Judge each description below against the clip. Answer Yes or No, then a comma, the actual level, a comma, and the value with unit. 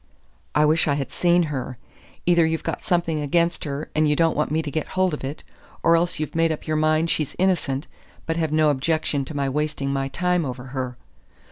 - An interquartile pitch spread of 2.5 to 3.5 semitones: Yes, average, 2.8 semitones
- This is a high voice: No, medium, 155 Hz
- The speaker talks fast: Yes, fast, 220 wpm